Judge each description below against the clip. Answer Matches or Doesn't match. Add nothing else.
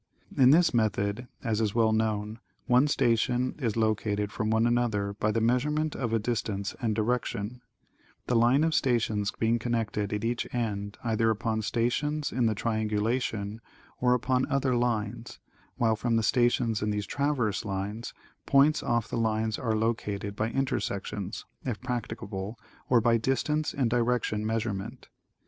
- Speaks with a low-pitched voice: Matches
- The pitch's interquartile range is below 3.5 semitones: Matches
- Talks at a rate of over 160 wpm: Doesn't match